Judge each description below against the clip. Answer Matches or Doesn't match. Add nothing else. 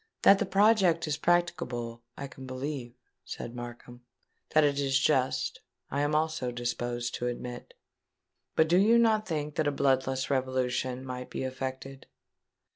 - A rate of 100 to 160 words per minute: Matches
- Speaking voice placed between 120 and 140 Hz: Matches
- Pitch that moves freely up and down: Doesn't match